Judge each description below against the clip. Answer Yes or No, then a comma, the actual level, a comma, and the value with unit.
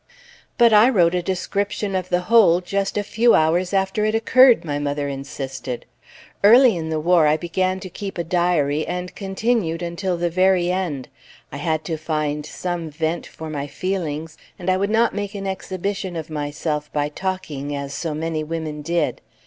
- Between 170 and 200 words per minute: Yes, average, 180 wpm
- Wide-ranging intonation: No, average, 3.9 semitones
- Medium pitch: Yes, medium, 175 Hz